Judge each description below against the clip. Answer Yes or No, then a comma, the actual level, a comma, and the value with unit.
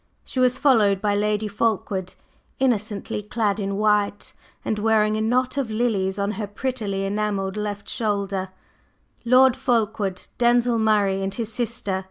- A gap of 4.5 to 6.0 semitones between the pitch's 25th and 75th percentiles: No, narrow, 2.6 semitones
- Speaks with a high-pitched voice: Yes, high, 210 Hz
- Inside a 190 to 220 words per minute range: No, average, 145 wpm